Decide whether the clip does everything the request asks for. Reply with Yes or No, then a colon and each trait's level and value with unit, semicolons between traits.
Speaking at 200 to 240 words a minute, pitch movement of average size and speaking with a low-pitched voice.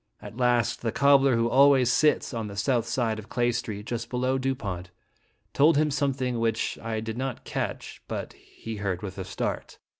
No: average, 185 wpm; average, 3.2 semitones; low, 120 Hz